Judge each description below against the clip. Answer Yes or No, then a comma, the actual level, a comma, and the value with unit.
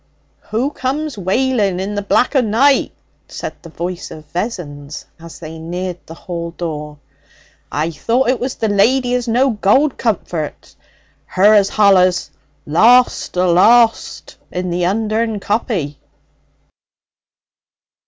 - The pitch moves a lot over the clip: Yes, wide, 5.7 semitones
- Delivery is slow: Yes, slow, 125 wpm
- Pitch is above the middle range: Yes, high, 200 Hz